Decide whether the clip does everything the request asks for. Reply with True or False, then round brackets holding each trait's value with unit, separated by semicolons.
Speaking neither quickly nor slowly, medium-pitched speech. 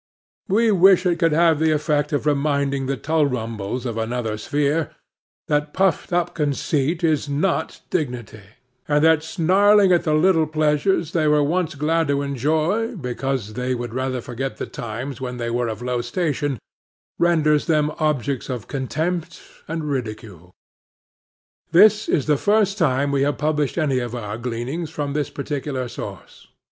True (155 wpm; 145 Hz)